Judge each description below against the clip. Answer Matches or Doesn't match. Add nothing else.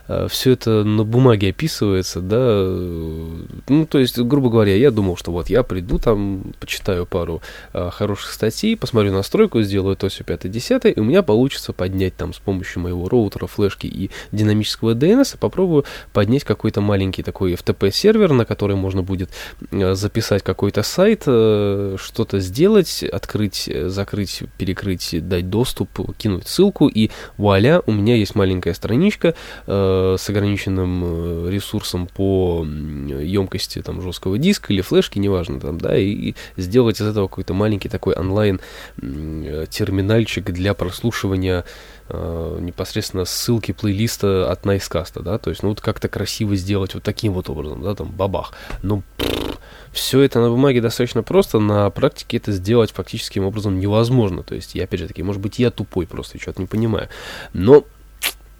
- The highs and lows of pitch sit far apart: Doesn't match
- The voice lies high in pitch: Doesn't match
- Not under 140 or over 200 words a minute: Matches